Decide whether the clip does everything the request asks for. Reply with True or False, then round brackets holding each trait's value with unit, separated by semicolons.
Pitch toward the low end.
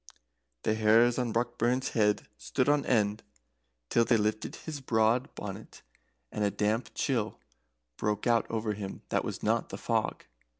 True (110 Hz)